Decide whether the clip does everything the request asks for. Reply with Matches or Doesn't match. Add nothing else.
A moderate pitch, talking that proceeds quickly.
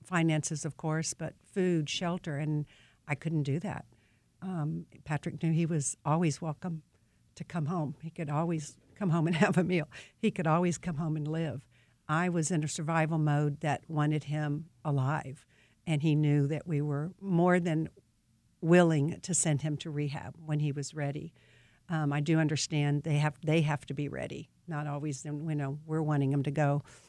Doesn't match